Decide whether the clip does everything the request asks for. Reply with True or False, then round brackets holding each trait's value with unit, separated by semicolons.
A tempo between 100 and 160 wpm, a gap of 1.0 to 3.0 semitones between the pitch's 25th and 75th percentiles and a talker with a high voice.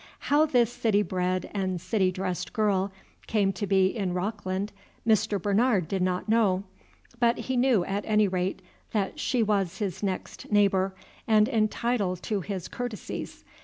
True (150 wpm; 2.7 semitones; 200 Hz)